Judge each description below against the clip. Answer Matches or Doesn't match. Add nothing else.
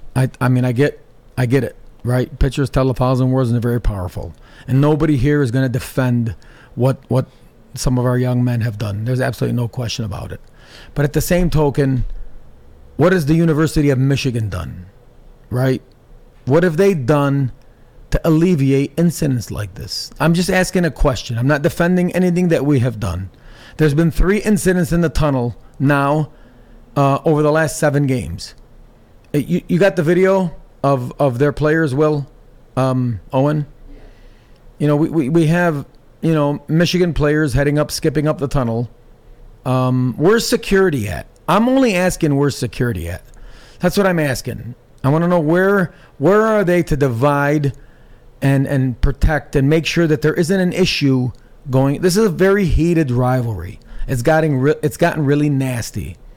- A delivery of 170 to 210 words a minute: Matches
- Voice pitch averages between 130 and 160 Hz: Matches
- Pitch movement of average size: Matches